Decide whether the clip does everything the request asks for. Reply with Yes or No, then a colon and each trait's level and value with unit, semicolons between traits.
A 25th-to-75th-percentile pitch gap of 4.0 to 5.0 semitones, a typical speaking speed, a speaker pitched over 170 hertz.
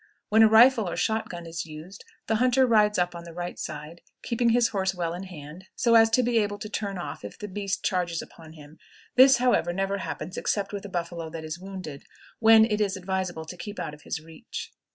No: average, 4.5 semitones; fast, 230 wpm; high, 190 Hz